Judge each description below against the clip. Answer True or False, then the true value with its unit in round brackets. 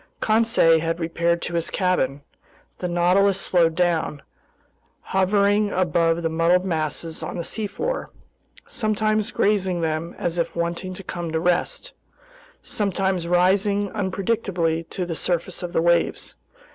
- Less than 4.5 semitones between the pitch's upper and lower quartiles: True (2.9 semitones)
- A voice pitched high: False (175 Hz)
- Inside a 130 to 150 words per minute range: True (135 wpm)